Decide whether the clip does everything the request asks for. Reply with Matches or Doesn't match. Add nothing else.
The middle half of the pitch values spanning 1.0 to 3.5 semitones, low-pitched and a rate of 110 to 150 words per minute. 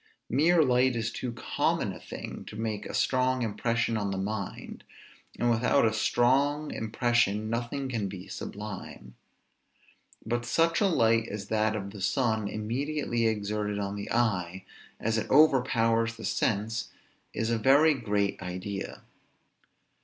Matches